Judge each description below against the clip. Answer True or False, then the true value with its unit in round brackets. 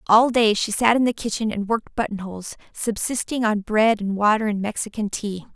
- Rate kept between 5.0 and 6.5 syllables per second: True (5.5 syllables/s)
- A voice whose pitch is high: True (215 Hz)